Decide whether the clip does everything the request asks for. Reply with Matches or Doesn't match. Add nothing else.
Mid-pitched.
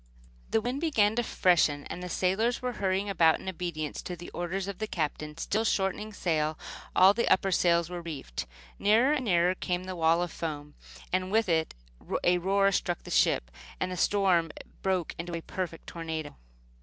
Matches